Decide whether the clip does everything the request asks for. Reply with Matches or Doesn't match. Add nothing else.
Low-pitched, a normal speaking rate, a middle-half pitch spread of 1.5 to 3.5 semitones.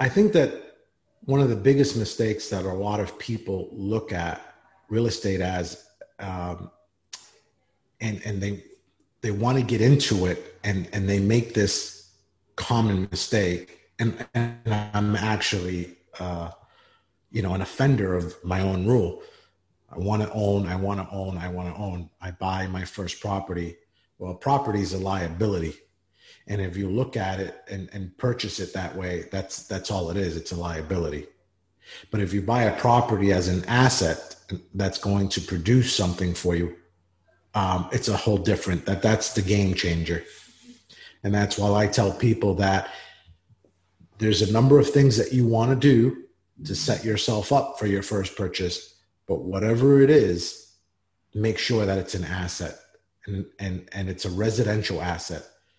Matches